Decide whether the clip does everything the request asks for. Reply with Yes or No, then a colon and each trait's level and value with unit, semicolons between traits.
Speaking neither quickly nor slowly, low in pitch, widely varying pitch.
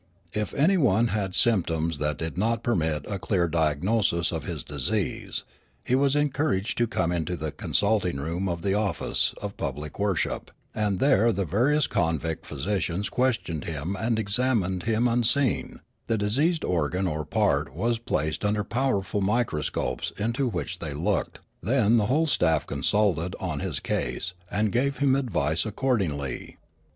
Yes: average, 160 wpm; low, 100 Hz; wide, 6.1 semitones